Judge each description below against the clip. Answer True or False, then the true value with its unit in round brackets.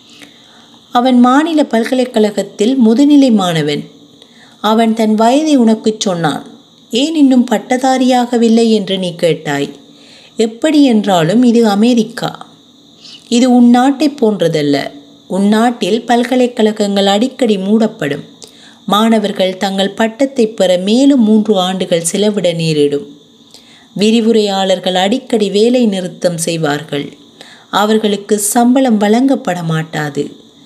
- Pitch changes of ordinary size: True (4.5 semitones)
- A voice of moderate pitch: False (225 Hz)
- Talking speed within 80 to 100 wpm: True (90 wpm)